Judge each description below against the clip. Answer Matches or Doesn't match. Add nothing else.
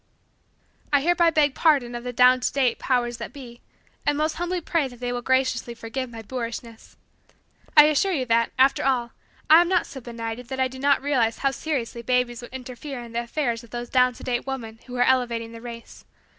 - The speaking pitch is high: Matches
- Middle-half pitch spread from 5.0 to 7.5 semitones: Doesn't match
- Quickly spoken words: Matches